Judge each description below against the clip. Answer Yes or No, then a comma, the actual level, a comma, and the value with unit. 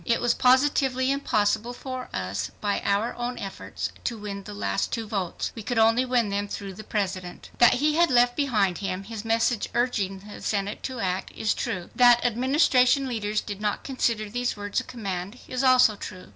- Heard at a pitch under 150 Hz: No, high, 225 Hz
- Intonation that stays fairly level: No, average, 3.8 semitones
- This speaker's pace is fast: No, average, 190 wpm